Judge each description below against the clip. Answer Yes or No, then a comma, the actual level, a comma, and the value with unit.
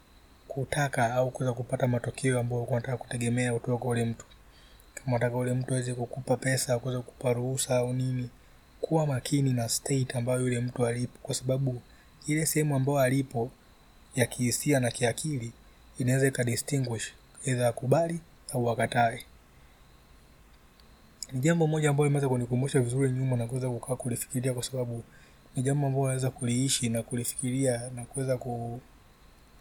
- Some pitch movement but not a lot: No, narrow, 2.0 semitones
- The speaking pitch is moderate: No, low, 125 Hz